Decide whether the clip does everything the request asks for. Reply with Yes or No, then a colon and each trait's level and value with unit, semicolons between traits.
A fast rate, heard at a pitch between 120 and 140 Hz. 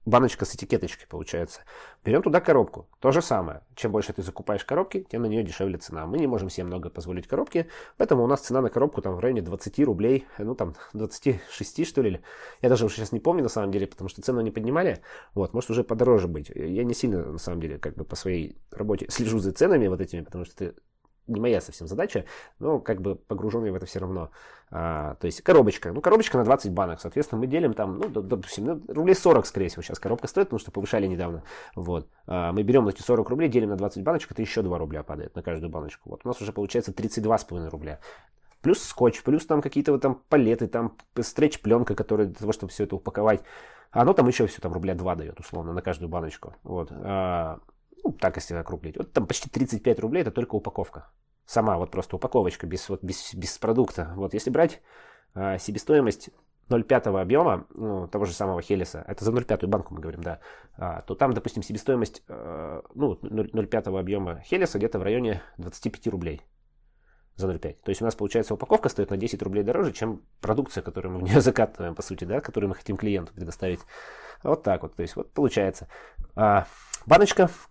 No: fast, 205 wpm; low, 100 Hz